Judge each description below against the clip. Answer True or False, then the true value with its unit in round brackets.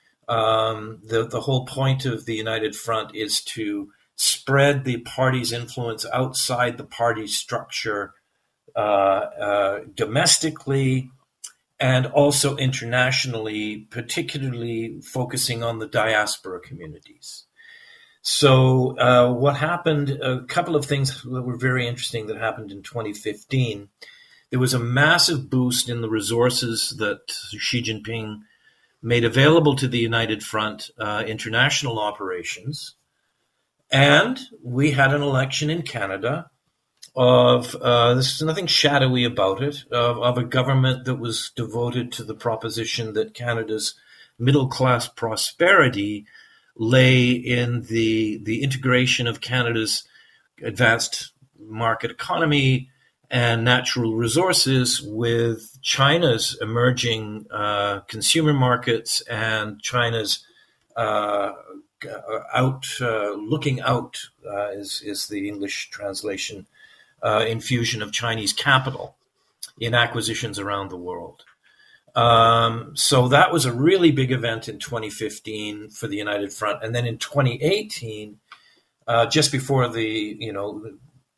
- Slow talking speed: True (120 wpm)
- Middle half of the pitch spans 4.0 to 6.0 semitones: False (3.2 semitones)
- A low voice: True (120 Hz)